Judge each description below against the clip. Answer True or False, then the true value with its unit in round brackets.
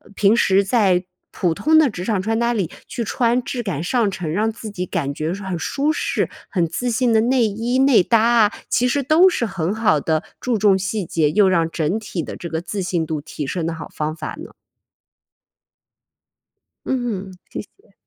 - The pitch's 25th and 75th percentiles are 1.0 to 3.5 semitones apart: False (5.4 semitones)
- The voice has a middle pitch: False (200 Hz)